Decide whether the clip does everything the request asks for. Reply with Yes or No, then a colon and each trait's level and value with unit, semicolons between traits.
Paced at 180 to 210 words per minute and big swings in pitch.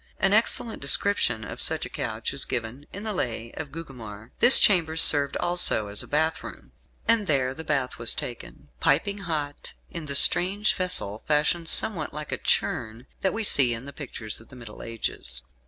Yes: average, 185 wpm; wide, 7.1 semitones